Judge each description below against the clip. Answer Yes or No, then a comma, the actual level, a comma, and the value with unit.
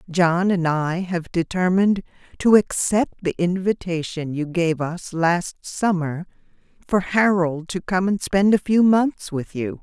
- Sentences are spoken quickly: No, average, 155 wpm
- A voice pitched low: No, medium, 180 Hz